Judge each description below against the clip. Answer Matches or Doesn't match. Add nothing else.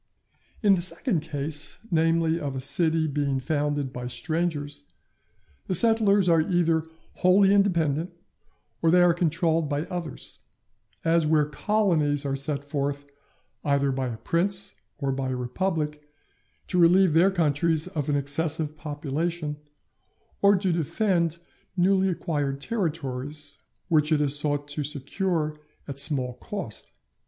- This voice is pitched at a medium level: Matches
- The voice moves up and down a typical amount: Matches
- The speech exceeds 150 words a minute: Doesn't match